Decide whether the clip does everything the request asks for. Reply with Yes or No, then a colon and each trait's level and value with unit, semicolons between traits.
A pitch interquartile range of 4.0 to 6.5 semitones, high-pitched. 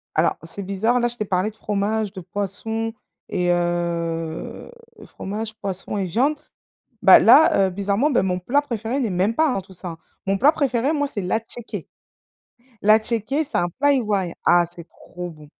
Yes: average, 4.7 semitones; high, 205 Hz